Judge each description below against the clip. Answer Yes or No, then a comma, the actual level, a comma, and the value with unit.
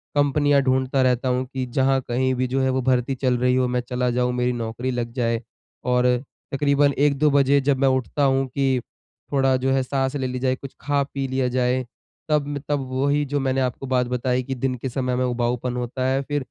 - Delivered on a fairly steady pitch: Yes, narrow, 1.5 semitones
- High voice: No, low, 130 Hz